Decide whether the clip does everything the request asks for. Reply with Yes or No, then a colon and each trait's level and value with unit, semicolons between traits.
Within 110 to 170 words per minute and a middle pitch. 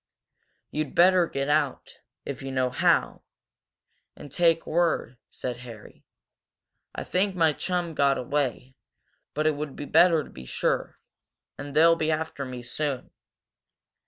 Yes: average, 140 wpm; medium, 145 Hz